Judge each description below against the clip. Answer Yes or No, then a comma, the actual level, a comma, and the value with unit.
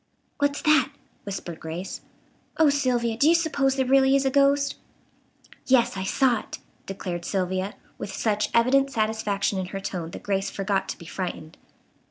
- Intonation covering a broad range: Yes, wide, 6.0 semitones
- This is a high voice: Yes, high, 225 Hz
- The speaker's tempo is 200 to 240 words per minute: No, average, 165 wpm